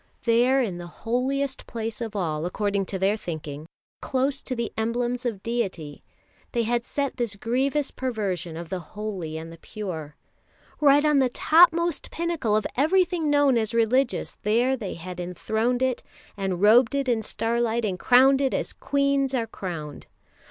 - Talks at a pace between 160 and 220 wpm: Yes, average, 165 wpm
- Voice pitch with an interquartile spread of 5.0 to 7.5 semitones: Yes, wide, 5.5 semitones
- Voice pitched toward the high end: Yes, high, 230 Hz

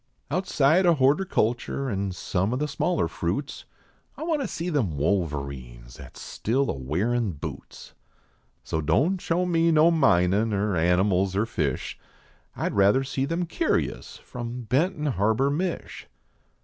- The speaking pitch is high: No, low, 120 Hz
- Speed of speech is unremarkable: Yes, average, 150 wpm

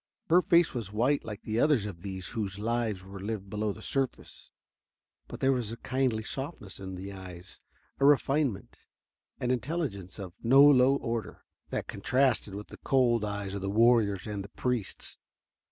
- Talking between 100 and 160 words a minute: No, average, 170 wpm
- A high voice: No, low, 110 Hz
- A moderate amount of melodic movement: Yes, average, 4.7 semitones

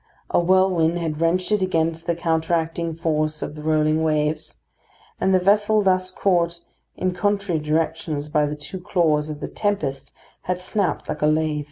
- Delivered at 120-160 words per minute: No, average, 170 wpm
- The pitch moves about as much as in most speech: Yes, average, 3.1 semitones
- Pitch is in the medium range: Yes, medium, 165 Hz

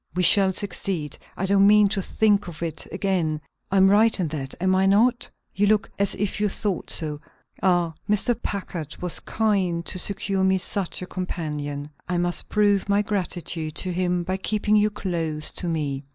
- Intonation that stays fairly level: No, average, 3.2 semitones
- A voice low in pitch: No, medium, 185 Hz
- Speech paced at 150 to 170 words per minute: No, average, 180 wpm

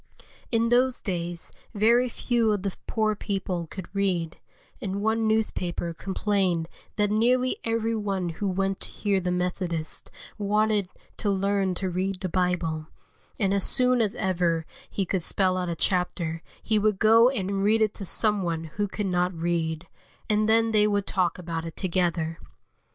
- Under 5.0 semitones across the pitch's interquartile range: Yes, average, 3.3 semitones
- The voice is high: Yes, high, 195 Hz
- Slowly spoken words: No, average, 165 wpm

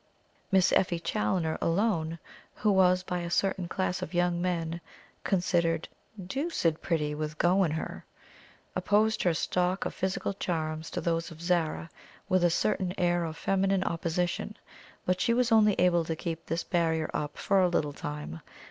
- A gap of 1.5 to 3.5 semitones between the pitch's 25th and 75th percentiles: Yes, narrow, 2.4 semitones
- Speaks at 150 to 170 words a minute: Yes, average, 165 wpm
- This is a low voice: No, medium, 175 Hz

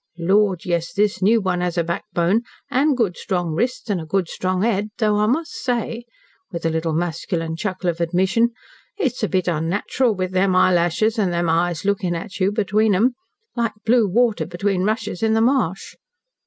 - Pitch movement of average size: Yes, average, 4.1 semitones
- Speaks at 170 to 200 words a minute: Yes, average, 185 wpm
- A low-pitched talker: No, high, 190 Hz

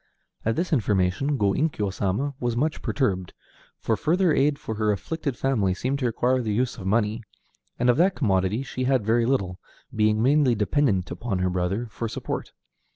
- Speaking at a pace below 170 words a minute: No, average, 180 wpm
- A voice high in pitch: No, low, 115 Hz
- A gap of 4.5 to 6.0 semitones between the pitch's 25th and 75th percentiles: Yes, average, 5.1 semitones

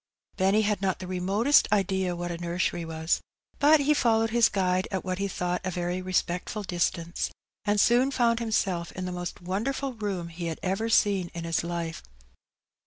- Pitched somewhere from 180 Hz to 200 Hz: Yes, medium, 185 Hz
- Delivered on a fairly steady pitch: No, average, 3.6 semitones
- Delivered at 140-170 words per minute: No, average, 180 wpm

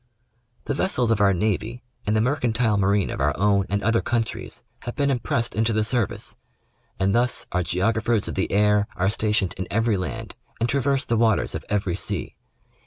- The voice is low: Yes, low, 110 Hz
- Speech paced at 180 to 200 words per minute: Yes, average, 185 wpm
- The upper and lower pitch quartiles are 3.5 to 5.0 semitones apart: No, average, 2.8 semitones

